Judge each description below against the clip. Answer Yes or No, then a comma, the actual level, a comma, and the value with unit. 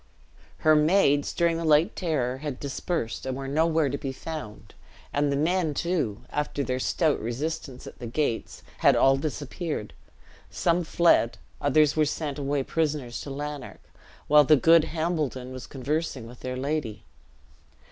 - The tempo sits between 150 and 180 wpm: Yes, average, 155 wpm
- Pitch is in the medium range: Yes, medium, 145 Hz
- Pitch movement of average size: Yes, average, 3.2 semitones